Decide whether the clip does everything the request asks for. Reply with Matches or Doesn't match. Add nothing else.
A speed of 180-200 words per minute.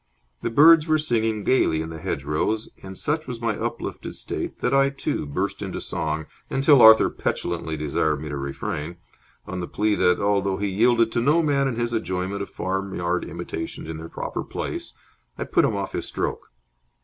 Matches